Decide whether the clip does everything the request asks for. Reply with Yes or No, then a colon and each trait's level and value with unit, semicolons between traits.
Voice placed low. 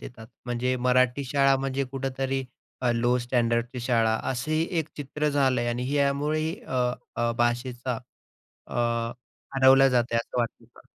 Yes: low, 130 Hz